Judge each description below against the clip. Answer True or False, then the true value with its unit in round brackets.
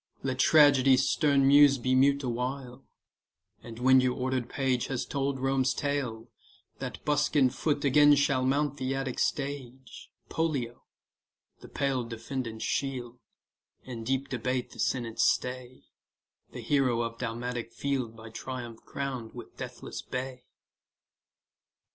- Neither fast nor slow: False (130 wpm)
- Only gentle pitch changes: True (2.2 semitones)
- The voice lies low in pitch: True (130 Hz)